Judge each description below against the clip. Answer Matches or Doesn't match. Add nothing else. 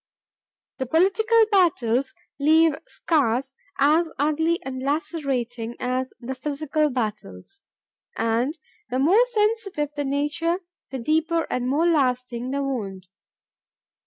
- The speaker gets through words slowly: Matches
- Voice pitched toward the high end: Matches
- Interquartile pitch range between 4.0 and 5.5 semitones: Matches